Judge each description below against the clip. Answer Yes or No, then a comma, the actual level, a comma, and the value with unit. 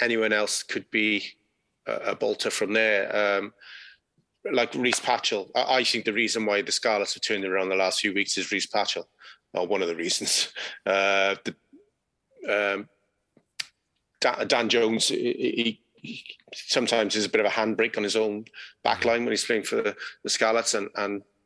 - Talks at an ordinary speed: Yes, average, 185 wpm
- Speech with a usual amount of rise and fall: No, narrow, 1.7 semitones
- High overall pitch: No, low, 105 Hz